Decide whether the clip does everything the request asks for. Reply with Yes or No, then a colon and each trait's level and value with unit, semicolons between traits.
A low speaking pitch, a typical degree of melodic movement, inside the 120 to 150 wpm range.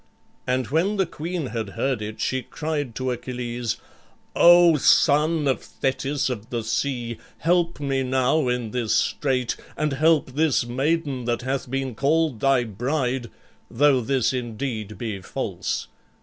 Yes: low, 130 Hz; average, 3.6 semitones; average, 145 wpm